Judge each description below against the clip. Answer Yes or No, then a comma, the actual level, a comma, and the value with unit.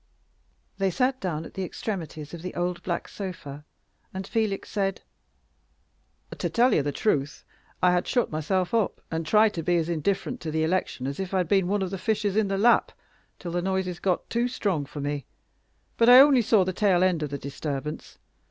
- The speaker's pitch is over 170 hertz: Yes, medium, 185 Hz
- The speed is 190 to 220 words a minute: Yes, average, 200 wpm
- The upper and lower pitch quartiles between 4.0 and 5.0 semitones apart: Yes, average, 4.3 semitones